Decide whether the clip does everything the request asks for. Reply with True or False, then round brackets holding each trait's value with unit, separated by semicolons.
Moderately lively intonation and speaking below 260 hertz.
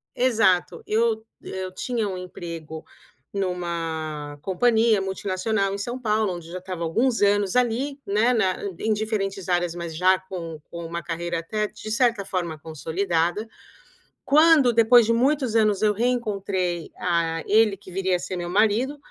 True (4.3 semitones; 195 Hz)